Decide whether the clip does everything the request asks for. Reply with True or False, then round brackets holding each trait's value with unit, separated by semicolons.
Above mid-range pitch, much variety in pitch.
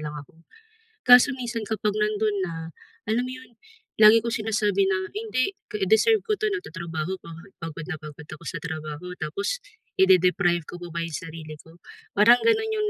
True (195 Hz; 6.4 semitones)